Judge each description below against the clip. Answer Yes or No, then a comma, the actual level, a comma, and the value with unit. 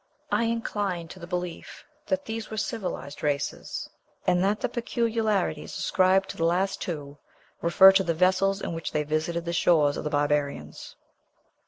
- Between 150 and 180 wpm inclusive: Yes, average, 165 wpm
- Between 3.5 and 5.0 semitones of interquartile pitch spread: Yes, average, 4.6 semitones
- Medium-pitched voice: Yes, medium, 180 Hz